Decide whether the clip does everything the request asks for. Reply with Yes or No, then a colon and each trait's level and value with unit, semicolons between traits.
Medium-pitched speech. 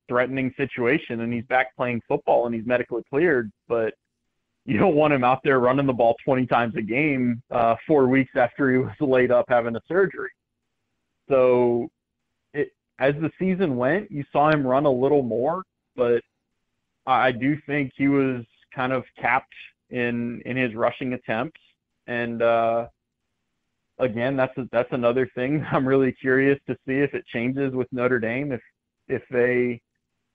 No: low, 125 Hz